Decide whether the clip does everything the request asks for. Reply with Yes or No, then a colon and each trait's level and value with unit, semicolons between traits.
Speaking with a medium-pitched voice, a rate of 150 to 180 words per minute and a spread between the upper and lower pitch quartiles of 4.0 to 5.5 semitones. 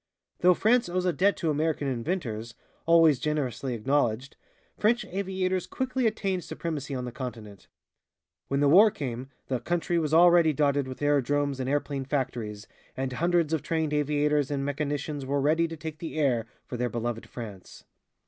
Yes: medium, 145 Hz; average, 165 wpm; average, 4.4 semitones